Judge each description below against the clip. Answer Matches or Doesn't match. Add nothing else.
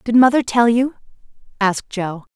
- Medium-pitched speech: Doesn't match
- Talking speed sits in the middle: Matches